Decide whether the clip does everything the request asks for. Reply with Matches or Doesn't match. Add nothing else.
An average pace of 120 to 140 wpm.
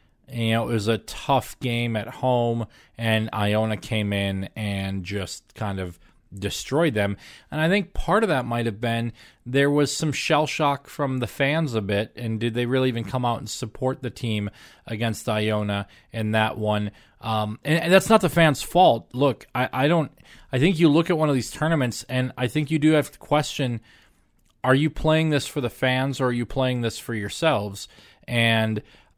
Doesn't match